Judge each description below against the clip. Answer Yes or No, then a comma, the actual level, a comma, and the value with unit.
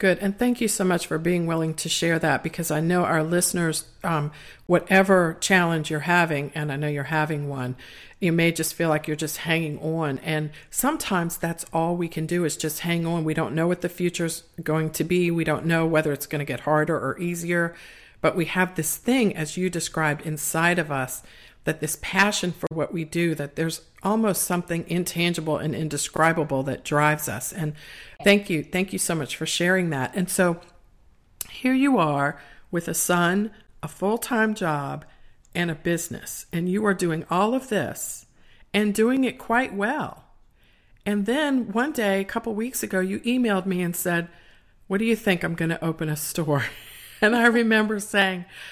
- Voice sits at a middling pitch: Yes, medium, 170 Hz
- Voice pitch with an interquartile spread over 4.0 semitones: No, average, 3.4 semitones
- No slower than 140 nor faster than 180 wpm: No, average, 195 wpm